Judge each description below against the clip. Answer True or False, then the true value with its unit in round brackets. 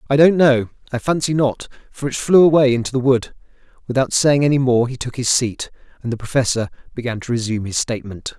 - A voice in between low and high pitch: False (130 Hz)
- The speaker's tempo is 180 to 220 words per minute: True (205 wpm)